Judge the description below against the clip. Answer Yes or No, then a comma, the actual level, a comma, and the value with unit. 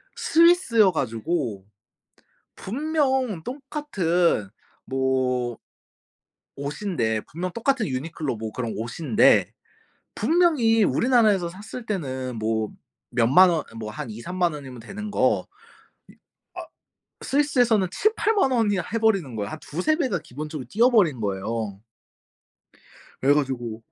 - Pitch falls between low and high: Yes, medium, 170 Hz